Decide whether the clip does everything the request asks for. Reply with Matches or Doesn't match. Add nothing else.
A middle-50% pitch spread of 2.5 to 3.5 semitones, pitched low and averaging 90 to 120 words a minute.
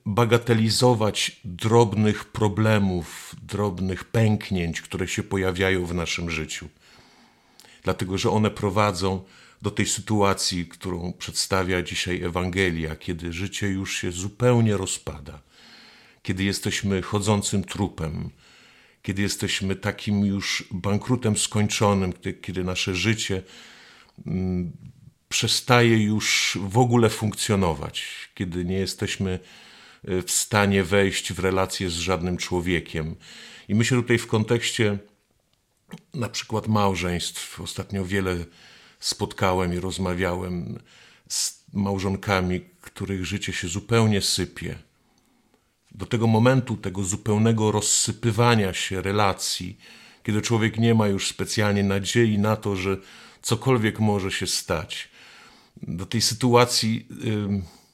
Matches